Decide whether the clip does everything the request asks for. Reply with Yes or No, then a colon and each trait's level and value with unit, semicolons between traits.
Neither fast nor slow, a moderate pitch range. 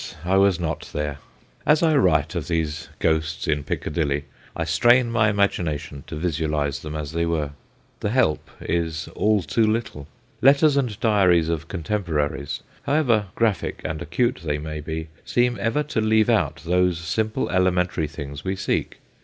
No: average, 160 wpm; wide, 5.9 semitones